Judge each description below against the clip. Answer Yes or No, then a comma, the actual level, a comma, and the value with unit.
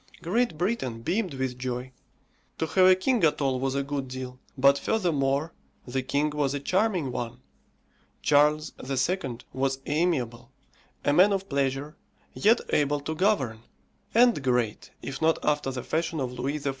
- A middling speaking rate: Yes, average, 160 wpm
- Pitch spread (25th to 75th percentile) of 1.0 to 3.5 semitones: No, average, 4.3 semitones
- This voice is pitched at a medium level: Yes, medium, 145 Hz